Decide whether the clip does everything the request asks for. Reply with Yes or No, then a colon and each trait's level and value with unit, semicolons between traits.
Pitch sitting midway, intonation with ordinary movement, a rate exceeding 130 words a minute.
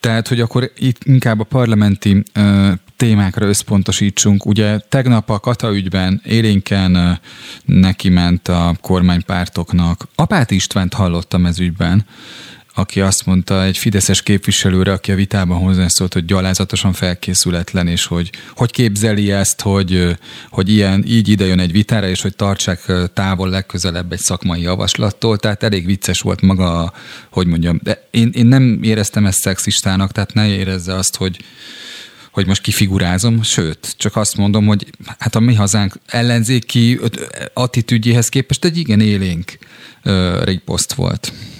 No: low, 100 Hz; average, 3.0 semitones; average, 140 wpm